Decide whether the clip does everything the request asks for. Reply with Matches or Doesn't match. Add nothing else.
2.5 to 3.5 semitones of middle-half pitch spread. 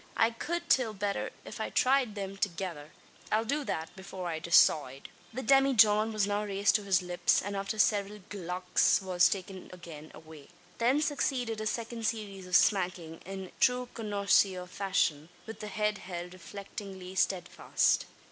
Matches